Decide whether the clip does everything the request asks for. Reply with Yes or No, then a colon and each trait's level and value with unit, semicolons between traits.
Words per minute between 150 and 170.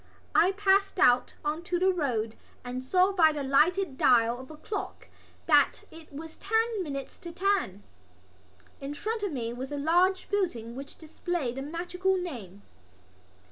Yes: average, 160 wpm